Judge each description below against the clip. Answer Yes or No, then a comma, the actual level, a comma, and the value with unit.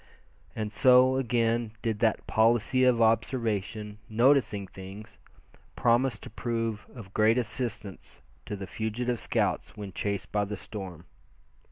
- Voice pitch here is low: Yes, low, 110 Hz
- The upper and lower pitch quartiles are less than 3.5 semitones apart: Yes, narrow, 2.5 semitones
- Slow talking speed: Yes, slow, 130 wpm